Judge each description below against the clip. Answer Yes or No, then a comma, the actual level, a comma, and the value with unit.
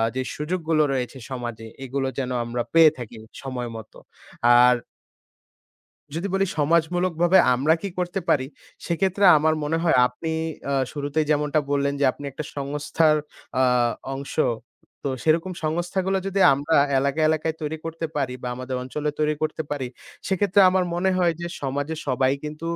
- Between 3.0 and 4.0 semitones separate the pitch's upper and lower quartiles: Yes, average, 3.7 semitones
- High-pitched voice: No, medium, 155 Hz